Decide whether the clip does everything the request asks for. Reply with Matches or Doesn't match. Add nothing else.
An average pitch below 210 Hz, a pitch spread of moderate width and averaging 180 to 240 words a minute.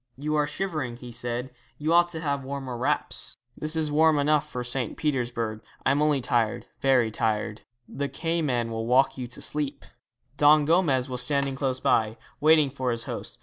Matches